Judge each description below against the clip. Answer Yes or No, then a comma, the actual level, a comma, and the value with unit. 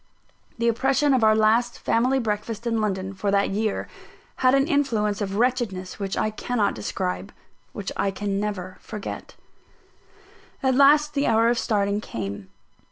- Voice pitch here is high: Yes, high, 215 Hz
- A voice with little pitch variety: No, average, 3.8 semitones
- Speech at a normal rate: Yes, average, 155 wpm